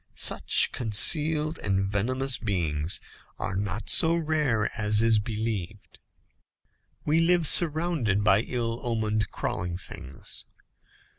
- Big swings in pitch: Yes, wide, 6.9 semitones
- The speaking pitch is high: No, low, 110 Hz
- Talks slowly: Yes, slow, 105 wpm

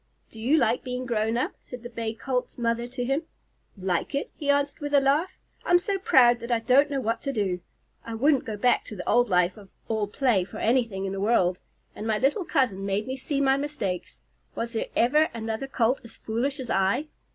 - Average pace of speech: No, fast, 220 wpm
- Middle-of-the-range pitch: No, high, 240 Hz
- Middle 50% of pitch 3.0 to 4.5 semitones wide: Yes, average, 3.9 semitones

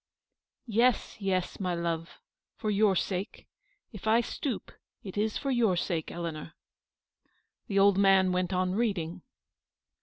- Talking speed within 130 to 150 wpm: Yes, average, 140 wpm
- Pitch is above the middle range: Yes, high, 195 Hz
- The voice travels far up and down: No, average, 3.0 semitones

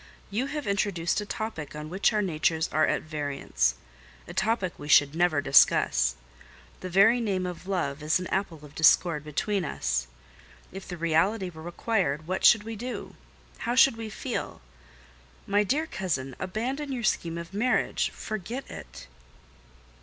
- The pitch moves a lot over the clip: Yes, wide, 6.0 semitones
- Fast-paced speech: No, average, 155 wpm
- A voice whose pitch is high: No, medium, 180 Hz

